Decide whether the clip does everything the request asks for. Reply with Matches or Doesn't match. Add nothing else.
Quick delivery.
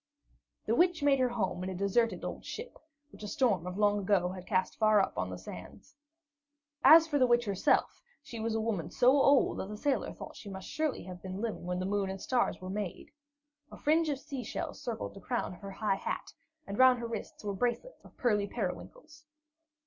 Matches